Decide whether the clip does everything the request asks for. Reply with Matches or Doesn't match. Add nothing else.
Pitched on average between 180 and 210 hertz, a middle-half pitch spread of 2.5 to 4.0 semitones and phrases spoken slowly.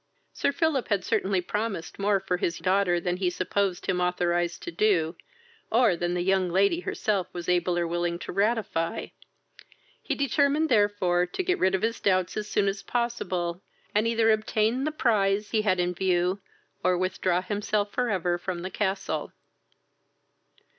Doesn't match